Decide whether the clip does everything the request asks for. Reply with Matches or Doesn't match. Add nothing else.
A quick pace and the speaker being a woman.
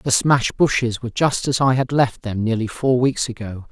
Doesn't match